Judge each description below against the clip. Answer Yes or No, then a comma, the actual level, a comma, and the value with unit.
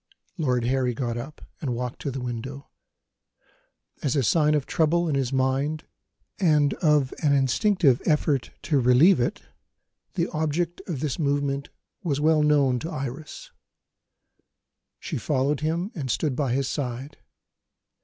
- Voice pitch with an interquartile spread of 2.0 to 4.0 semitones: Yes, average, 2.9 semitones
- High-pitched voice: No, medium, 140 Hz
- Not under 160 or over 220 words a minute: No, average, 145 wpm